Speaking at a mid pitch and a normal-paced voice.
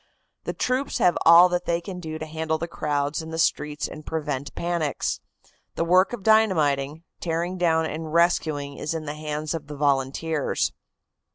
Yes: medium, 160 Hz; average, 175 wpm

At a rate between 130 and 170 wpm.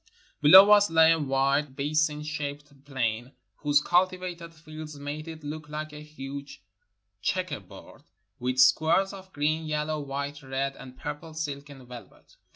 Yes: average, 150 wpm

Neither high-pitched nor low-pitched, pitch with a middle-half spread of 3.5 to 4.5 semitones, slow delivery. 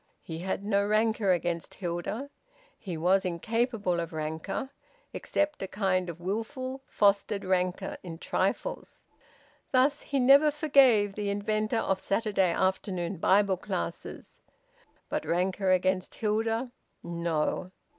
No: high, 195 Hz; average, 3.9 semitones; slow, 120 wpm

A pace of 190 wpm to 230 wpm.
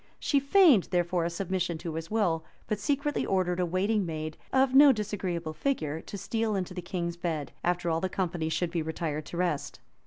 Yes: average, 195 wpm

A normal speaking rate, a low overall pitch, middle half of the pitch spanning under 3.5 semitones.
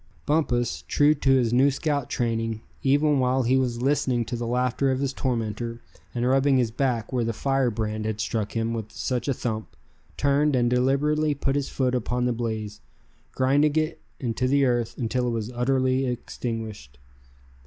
Yes: average, 175 wpm; low, 125 Hz; average, 2.8 semitones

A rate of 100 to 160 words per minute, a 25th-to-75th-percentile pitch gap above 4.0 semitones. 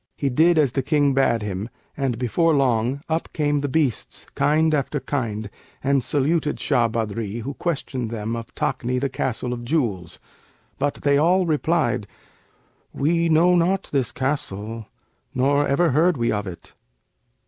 Yes: average, 155 wpm; average, 4.7 semitones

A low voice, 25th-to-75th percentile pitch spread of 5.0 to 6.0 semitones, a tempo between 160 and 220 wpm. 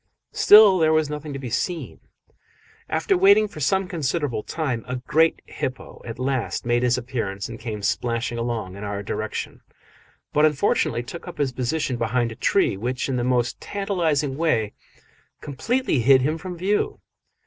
Yes: low, 130 Hz; average, 5.3 semitones; average, 165 wpm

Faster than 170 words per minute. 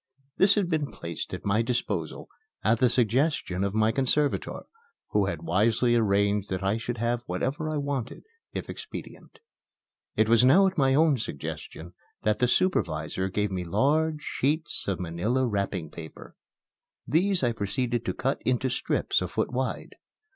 No: average, 160 wpm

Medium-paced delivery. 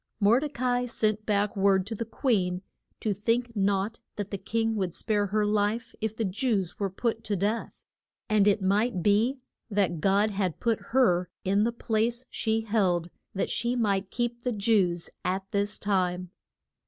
Yes: average, 180 wpm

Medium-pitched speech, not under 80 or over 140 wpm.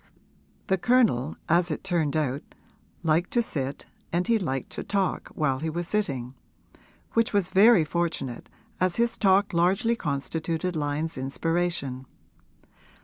Yes: medium, 170 Hz; slow, 135 wpm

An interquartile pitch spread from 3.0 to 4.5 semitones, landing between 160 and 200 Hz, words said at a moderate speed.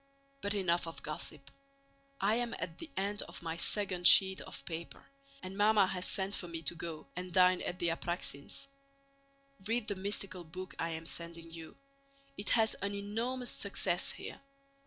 Yes: average, 3.3 semitones; medium, 185 Hz; average, 170 wpm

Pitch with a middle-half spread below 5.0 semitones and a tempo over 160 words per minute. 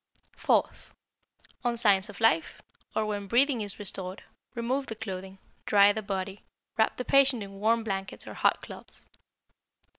No: average, 3.0 semitones; average, 150 wpm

